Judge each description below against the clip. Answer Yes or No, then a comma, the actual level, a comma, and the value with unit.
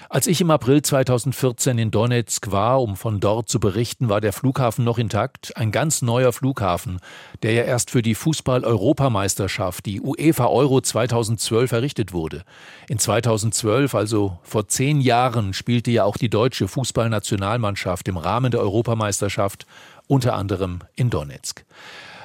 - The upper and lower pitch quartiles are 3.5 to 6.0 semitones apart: Yes, average, 3.9 semitones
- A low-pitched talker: Yes, low, 115 Hz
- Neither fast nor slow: Yes, average, 150 wpm